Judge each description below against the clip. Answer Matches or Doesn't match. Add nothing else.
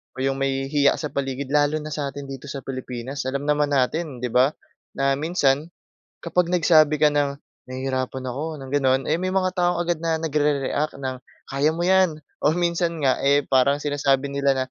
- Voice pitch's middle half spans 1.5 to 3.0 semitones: Matches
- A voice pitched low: Doesn't match